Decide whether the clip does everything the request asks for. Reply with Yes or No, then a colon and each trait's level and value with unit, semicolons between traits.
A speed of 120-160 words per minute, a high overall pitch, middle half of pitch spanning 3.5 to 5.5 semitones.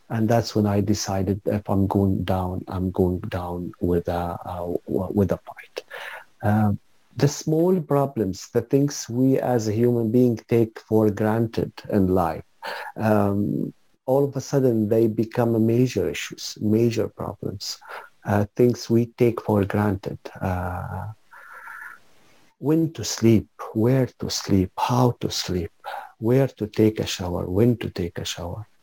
No: average, 150 wpm; low, 110 Hz; average, 3.8 semitones